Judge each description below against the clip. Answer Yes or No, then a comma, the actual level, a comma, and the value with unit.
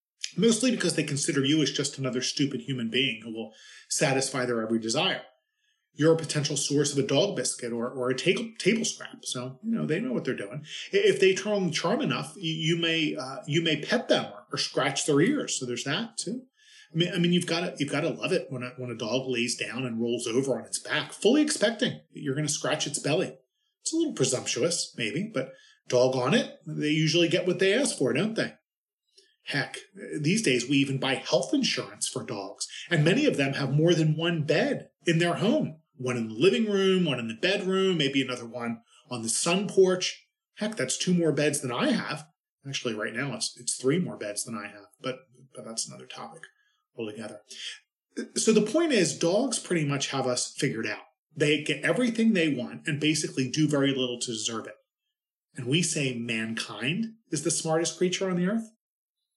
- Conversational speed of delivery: No, fast, 210 wpm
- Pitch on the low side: No, medium, 155 Hz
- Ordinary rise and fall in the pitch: No, wide, 6.7 semitones